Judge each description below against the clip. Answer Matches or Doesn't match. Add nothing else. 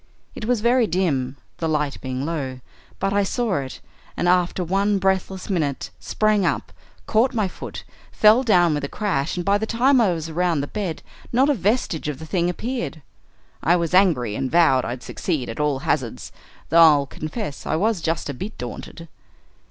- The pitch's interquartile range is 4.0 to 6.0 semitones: Matches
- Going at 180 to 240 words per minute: Matches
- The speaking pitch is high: Doesn't match